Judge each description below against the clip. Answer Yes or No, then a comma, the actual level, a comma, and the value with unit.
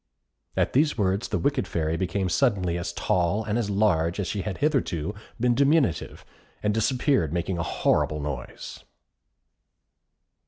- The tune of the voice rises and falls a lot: Yes, wide, 5.9 semitones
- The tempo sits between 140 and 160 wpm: Yes, average, 145 wpm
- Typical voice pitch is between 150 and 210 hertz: No, low, 100 Hz